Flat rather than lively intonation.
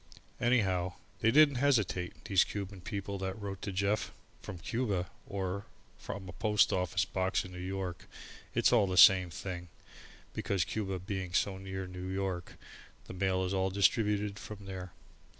Yes: narrow, 1.7 semitones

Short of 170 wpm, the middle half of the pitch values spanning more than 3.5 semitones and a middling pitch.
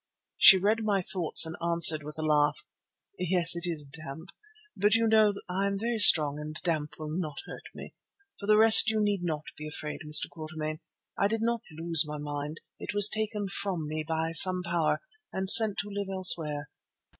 No: average, 190 wpm; average, 4.7 semitones; medium, 170 Hz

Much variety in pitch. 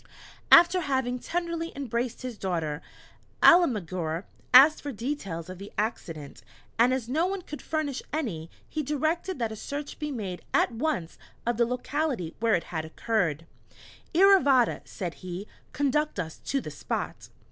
Yes: wide, 8.4 semitones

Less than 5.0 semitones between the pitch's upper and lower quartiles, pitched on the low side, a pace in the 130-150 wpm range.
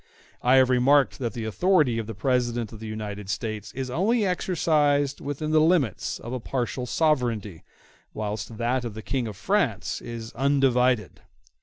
No: average, 4.4 semitones; low, 125 Hz; average, 165 wpm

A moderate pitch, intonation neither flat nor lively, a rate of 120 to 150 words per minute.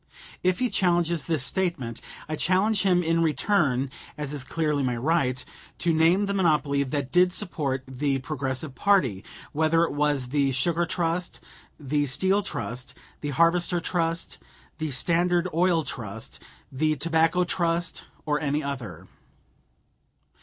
Yes: medium, 155 Hz; average, 4.2 semitones; average, 140 wpm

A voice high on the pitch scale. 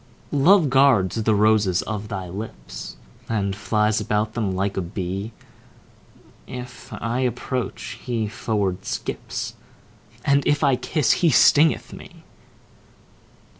No: low, 110 Hz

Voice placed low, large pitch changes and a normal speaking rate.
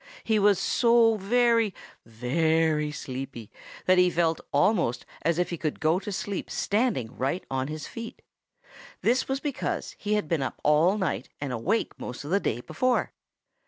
No: medium, 170 Hz; wide, 6.9 semitones; average, 165 wpm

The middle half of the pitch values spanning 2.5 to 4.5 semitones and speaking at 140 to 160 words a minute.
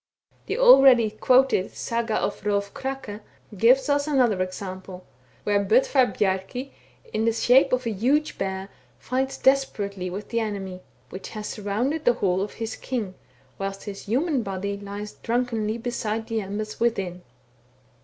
Yes: average, 4.2 semitones; average, 145 wpm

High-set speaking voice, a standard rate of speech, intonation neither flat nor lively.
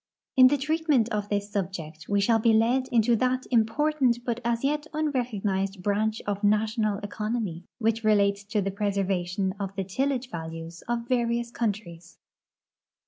Yes: high, 215 Hz; average, 155 wpm; average, 3.3 semitones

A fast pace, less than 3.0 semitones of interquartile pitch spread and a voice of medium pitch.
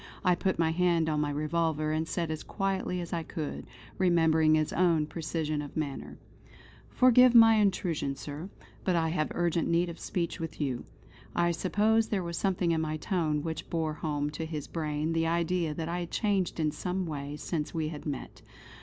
No: average, 190 wpm; narrow, 2.5 semitones; medium, 165 Hz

